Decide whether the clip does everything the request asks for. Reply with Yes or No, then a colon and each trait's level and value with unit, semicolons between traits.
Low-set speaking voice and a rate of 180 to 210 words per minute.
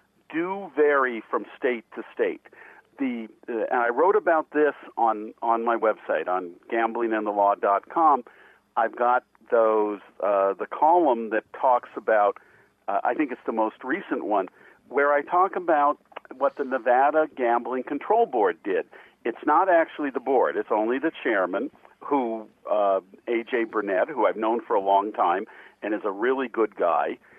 No: low, 130 Hz; average, 160 wpm